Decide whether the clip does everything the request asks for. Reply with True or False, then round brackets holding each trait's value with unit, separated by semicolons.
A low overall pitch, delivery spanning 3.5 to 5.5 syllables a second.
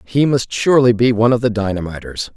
False (115 Hz; 6.2 syllables/s)